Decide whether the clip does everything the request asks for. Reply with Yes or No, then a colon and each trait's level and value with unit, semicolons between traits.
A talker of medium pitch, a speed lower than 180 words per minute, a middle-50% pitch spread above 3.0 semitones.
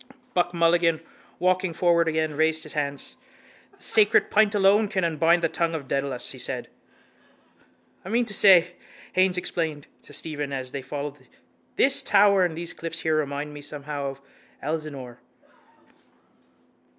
Yes: medium, 165 Hz; average, 150 wpm; average, 3.8 semitones